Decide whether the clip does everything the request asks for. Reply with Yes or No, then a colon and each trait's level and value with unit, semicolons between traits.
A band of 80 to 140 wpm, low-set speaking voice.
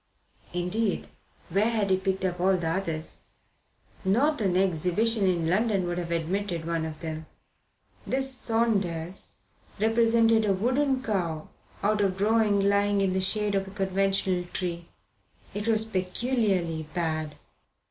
No: slow, 135 wpm; high, 195 Hz